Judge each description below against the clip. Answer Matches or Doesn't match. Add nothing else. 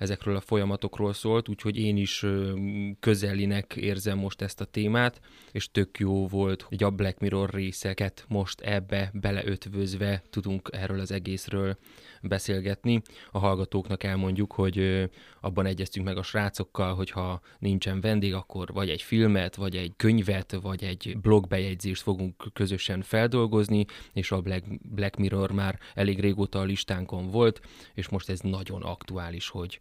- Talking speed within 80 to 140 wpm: Doesn't match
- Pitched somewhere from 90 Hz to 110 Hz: Matches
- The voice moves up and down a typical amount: Doesn't match